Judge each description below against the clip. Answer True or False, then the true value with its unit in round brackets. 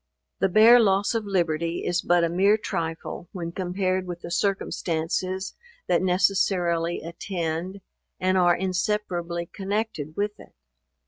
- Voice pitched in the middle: True (180 Hz)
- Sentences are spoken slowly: True (130 wpm)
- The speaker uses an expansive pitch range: False (2.4 semitones)